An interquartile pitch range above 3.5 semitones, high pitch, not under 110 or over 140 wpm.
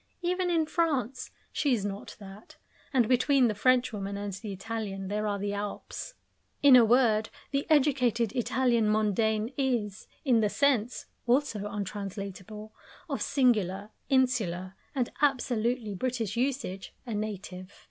Yes: average, 4.0 semitones; high, 225 Hz; slow, 135 wpm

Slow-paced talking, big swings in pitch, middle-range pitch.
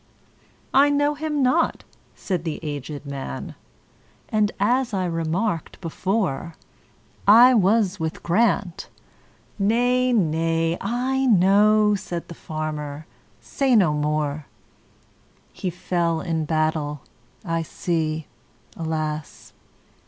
Yes: slow, 85 wpm; wide, 5.8 semitones; medium, 175 Hz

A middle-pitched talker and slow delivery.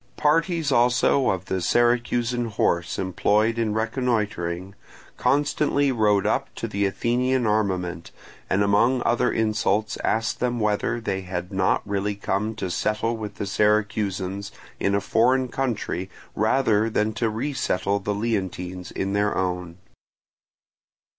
No: low, 105 Hz; slow, 130 wpm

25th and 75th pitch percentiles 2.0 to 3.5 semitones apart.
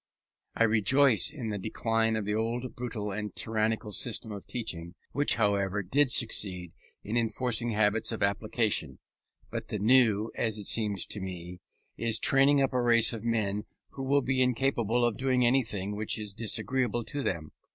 Yes: average, 2.9 semitones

